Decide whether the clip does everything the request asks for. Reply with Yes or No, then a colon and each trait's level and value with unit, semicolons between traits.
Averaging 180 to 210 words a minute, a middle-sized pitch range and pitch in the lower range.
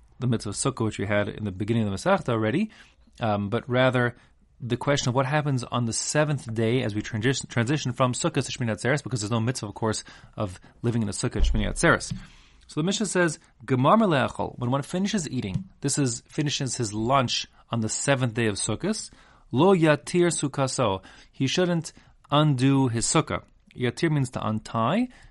Yes: average, 190 wpm; average, 4.7 semitones; low, 125 Hz